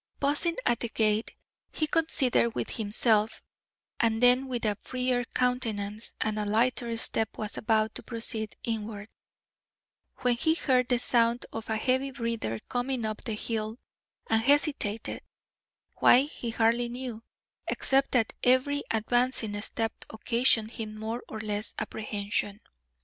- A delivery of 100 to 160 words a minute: Yes, average, 140 wpm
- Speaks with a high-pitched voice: Yes, high, 230 Hz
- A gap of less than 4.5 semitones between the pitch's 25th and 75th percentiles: Yes, narrow, 2.5 semitones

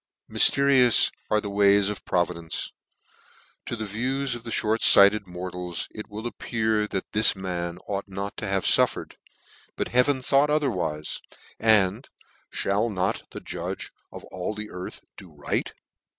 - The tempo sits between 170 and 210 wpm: No, average, 150 wpm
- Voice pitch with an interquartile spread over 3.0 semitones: Yes, average, 3.8 semitones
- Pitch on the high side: No, low, 105 Hz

